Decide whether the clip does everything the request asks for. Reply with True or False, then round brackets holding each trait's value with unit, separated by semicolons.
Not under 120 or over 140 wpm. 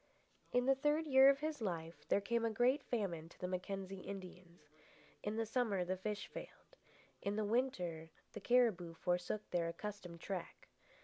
False (170 wpm)